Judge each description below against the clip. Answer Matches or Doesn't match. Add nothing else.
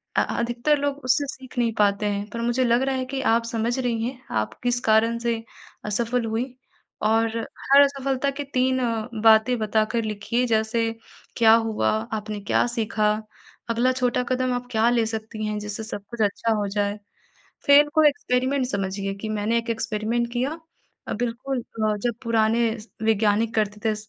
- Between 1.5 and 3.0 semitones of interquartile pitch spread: Matches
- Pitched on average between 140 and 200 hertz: Doesn't match